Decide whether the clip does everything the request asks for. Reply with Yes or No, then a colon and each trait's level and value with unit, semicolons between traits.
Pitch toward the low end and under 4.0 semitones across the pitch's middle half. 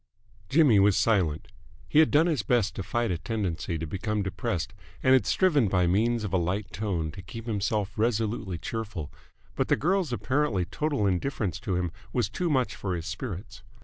No: low, 105 Hz; average, 4.6 semitones